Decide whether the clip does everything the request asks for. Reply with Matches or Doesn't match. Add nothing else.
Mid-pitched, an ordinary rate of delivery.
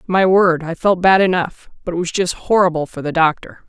Doesn't match